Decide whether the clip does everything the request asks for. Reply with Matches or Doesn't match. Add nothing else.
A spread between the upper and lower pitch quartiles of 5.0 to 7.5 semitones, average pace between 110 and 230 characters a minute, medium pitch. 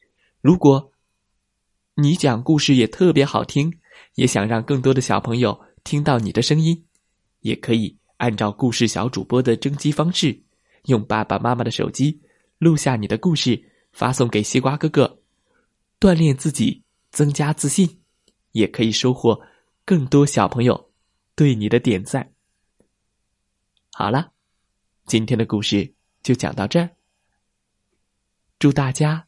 Doesn't match